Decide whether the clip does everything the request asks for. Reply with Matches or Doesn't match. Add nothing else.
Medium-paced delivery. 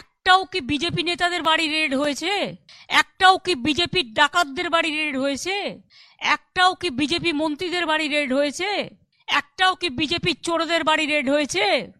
Doesn't match